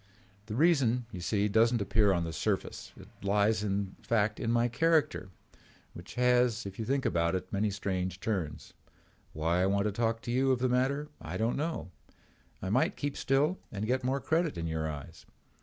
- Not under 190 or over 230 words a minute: Yes, average, 195 wpm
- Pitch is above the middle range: No, low, 110 Hz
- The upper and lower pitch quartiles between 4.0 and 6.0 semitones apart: Yes, average, 5.1 semitones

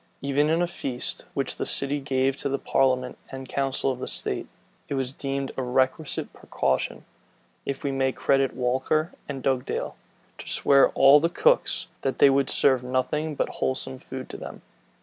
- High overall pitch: No, low, 135 Hz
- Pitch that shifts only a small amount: Yes, narrow, 1.2 semitones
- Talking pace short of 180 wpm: Yes, average, 170 wpm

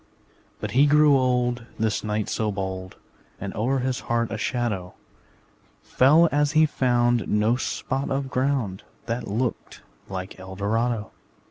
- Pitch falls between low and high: No, low, 120 Hz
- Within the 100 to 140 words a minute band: Yes, slow, 135 wpm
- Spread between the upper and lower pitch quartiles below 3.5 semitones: No, average, 3.9 semitones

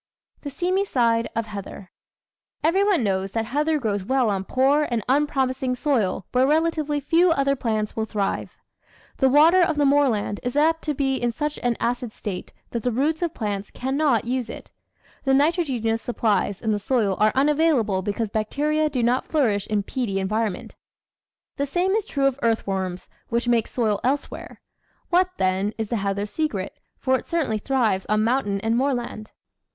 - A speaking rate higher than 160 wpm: Yes, average, 175 wpm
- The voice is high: Yes, high, 245 Hz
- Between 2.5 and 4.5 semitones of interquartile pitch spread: No, average, 5.3 semitones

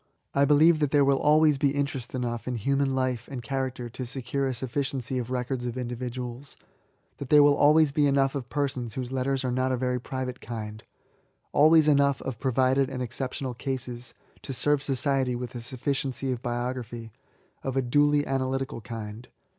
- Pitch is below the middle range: Yes, low, 130 Hz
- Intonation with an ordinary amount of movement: No, narrow, 2.2 semitones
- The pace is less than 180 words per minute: No, average, 185 wpm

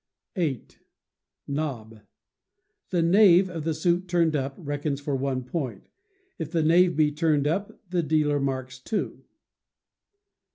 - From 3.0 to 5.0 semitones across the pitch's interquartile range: Yes, average, 3.7 semitones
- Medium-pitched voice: Yes, medium, 155 Hz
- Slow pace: Yes, slow, 130 wpm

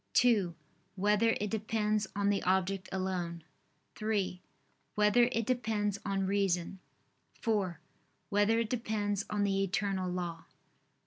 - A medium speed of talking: No, slow, 120 wpm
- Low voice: No, high, 200 Hz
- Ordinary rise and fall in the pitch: No, narrow, 2.2 semitones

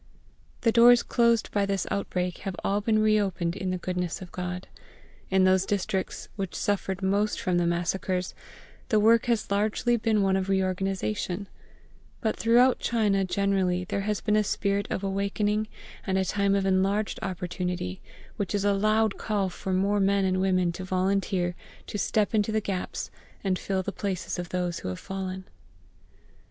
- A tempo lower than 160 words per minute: No, average, 170 wpm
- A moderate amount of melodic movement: No, narrow, 2.1 semitones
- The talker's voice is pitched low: No, high, 195 Hz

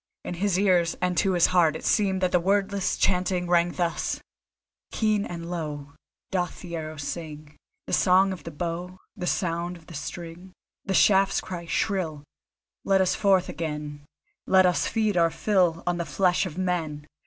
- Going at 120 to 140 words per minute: No, average, 175 wpm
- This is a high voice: No, medium, 175 Hz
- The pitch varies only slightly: Yes, narrow, 2.3 semitones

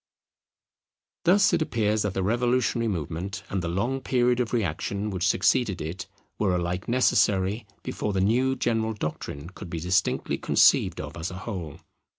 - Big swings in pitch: No, average, 4.7 semitones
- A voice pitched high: No, low, 100 Hz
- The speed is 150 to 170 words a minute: Yes, average, 160 wpm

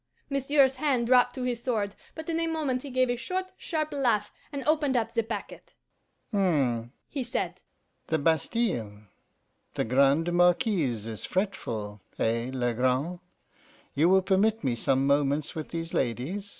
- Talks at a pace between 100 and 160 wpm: Yes, average, 150 wpm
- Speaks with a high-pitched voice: Yes, high, 195 Hz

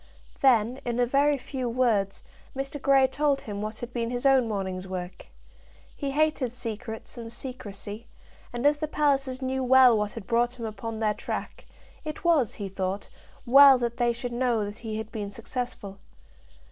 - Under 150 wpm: No, average, 175 wpm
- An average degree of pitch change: Yes, average, 3.6 semitones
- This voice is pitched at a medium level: No, high, 240 Hz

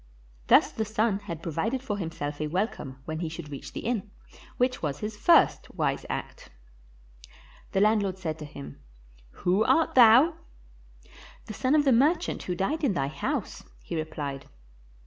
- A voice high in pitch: Yes, high, 195 Hz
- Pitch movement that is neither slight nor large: No, wide, 6.6 semitones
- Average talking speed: Yes, average, 165 wpm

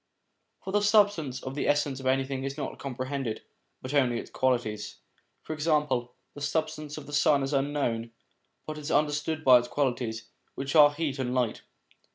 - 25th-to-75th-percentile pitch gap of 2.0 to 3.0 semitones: Yes, narrow, 2.6 semitones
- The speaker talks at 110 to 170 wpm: No, average, 180 wpm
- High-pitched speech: No, medium, 140 Hz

